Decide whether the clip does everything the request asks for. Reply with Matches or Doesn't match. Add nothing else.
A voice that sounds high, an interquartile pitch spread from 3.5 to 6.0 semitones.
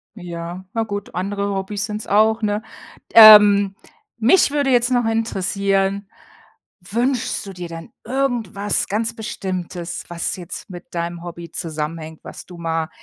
Matches